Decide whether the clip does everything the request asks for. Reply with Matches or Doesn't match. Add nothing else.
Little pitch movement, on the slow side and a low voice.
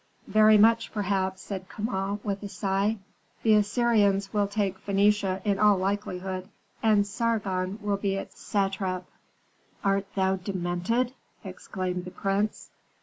Doesn't match